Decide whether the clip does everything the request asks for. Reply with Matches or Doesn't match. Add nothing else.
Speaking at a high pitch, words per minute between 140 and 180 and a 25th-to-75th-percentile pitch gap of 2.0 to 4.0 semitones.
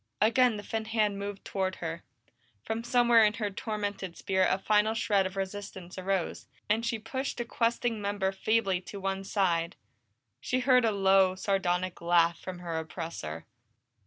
Matches